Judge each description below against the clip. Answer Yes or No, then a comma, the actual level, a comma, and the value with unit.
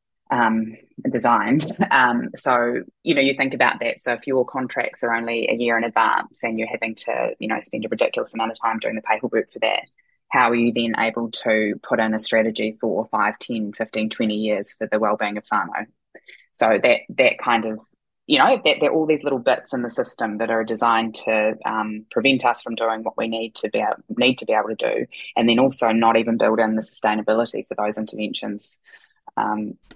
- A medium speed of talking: No, fast, 215 wpm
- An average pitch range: No, narrow, 1.4 semitones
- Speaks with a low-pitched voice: Yes, low, 115 Hz